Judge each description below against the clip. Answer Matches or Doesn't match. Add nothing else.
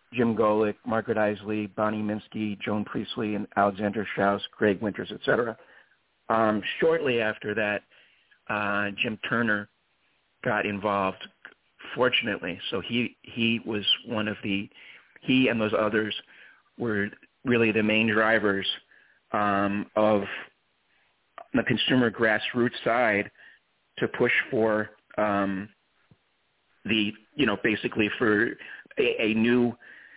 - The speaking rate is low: Matches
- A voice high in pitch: Doesn't match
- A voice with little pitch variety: Matches